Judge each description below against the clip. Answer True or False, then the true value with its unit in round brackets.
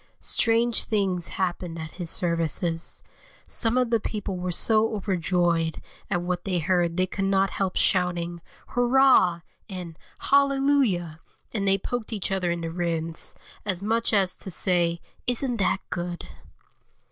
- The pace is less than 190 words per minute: True (145 wpm)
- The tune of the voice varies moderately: True (3.9 semitones)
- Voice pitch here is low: False (185 Hz)